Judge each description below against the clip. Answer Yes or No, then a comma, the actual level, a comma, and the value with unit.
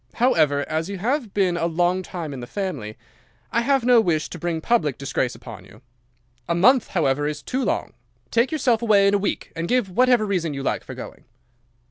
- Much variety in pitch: Yes, wide, 7.6 semitones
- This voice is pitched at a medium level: Yes, medium, 180 Hz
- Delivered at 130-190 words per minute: No, fast, 205 wpm